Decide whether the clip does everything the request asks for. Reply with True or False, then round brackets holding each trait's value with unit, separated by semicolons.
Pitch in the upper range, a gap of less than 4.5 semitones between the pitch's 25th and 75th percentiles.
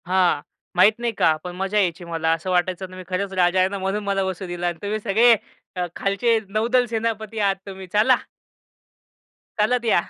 True (195 Hz; 3.0 semitones)